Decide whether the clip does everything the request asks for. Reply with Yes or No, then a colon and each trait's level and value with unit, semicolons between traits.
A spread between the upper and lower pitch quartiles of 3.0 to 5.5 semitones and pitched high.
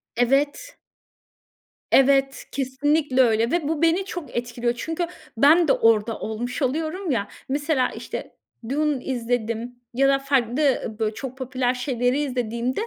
Yes: average, 3.5 semitones; very high, 260 Hz